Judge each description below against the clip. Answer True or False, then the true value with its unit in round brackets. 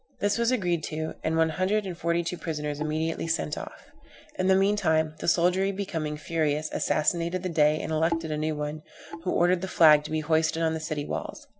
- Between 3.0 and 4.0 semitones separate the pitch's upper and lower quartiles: False (2.6 semitones)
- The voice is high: False (160 Hz)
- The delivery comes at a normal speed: False (210 wpm)